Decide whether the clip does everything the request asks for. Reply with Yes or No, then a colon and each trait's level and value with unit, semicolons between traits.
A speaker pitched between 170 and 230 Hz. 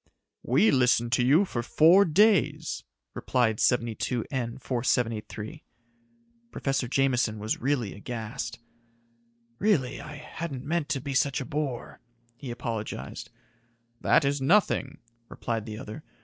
No: low, 130 Hz